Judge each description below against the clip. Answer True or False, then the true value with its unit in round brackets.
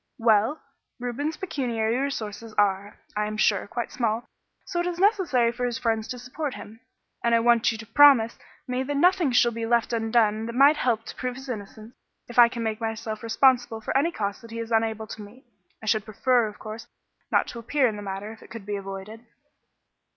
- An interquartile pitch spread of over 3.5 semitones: False (2.5 semitones)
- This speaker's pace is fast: True (210 wpm)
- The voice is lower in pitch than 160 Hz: False (230 Hz)